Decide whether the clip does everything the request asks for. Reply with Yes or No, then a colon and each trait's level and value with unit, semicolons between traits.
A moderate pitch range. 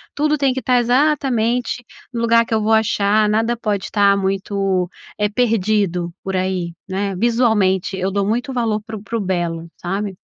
Yes: average, 3.4 semitones